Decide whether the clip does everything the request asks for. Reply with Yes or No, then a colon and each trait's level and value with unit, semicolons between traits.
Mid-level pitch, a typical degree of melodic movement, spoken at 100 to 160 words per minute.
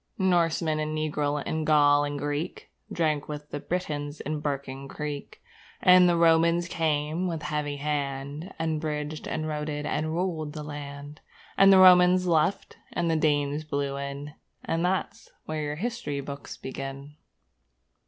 No: medium, 150 Hz; narrow, 2.2 semitones; average, 155 wpm